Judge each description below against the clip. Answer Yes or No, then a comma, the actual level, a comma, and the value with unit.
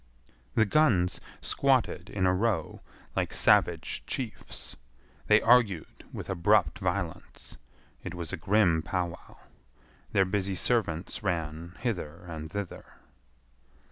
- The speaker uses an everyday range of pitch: Yes, average, 4.0 semitones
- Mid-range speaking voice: No, very low, 95 Hz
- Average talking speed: No, slow, 115 wpm